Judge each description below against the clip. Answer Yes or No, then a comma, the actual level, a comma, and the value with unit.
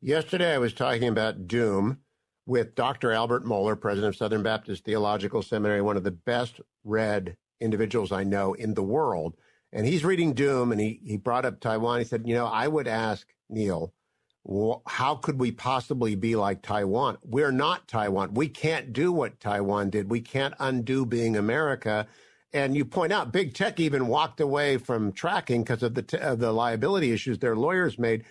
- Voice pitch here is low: Yes, low, 115 Hz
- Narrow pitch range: No, average, 4.0 semitones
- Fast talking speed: No, average, 190 wpm